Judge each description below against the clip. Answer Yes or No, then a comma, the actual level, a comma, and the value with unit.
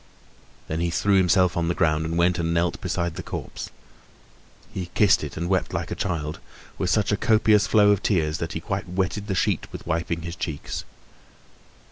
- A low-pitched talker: Yes, very low, 85 Hz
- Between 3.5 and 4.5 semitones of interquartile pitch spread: No, average, 2.9 semitones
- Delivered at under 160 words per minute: No, average, 195 wpm